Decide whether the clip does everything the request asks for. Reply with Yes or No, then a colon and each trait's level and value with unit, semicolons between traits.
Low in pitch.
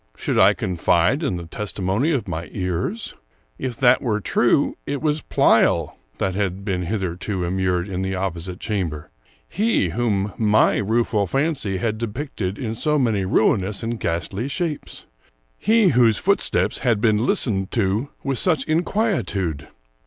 Yes: low, 105 Hz